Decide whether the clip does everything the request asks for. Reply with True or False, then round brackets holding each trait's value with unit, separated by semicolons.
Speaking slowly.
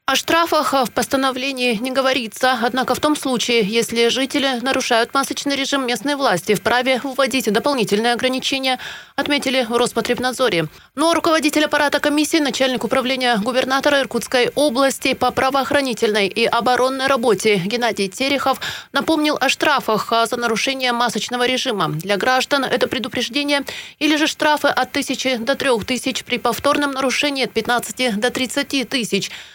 False (135 wpm)